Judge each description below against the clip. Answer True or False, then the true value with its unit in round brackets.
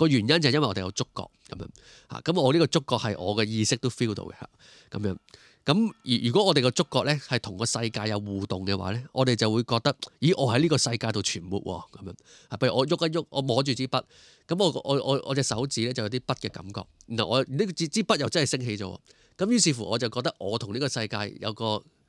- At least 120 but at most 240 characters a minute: False (360 characters per minute)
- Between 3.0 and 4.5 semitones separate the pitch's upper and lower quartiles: False (4.9 semitones)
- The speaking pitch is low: True (125 Hz)